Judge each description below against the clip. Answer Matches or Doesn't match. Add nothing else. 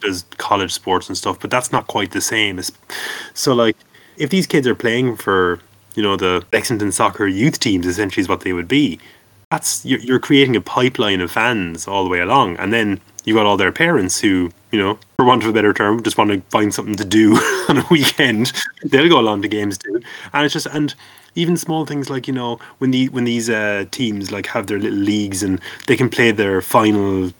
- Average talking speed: Doesn't match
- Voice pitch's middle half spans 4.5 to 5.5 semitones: Matches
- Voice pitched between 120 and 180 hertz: Doesn't match